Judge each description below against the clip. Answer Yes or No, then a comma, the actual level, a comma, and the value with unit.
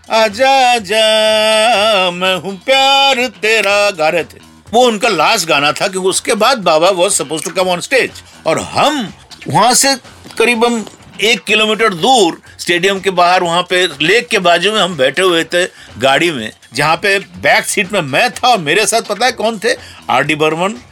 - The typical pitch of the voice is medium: No, high, 200 Hz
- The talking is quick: No, average, 180 wpm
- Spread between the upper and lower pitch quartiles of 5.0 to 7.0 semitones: No, average, 4.4 semitones